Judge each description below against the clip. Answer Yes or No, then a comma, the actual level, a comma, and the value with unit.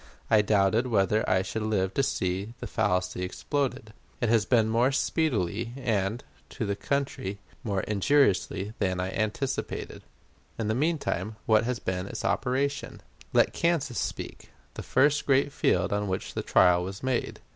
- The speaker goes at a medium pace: Yes, average, 160 wpm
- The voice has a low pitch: Yes, low, 110 Hz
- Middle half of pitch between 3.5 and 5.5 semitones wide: Yes, average, 5.2 semitones